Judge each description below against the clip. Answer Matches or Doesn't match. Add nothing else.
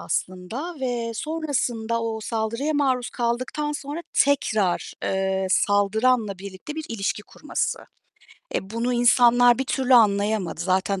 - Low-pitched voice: Doesn't match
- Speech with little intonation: Doesn't match